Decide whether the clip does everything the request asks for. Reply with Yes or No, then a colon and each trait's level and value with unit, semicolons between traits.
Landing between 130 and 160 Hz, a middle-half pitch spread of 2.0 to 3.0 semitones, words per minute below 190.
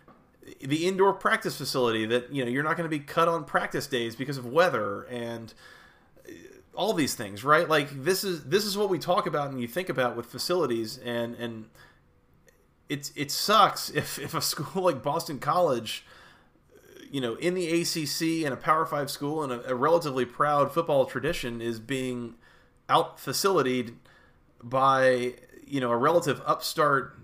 No: medium, 140 Hz; average, 5.2 semitones; average, 170 wpm